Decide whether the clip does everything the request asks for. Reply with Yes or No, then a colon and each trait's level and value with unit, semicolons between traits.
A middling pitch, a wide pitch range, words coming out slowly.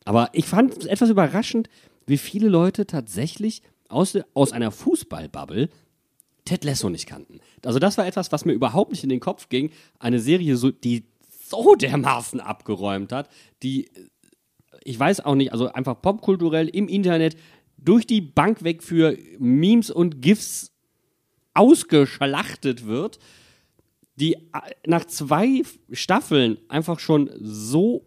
No: medium, 160 Hz; wide, 6.5 semitones; average, 140 wpm